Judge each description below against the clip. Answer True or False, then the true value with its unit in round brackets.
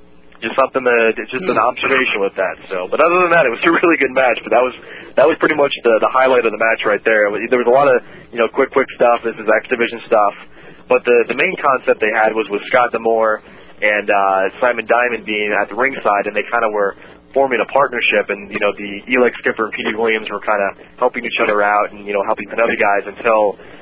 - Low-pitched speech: True (110 Hz)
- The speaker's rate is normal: False (245 wpm)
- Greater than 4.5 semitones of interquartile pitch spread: False (3.1 semitones)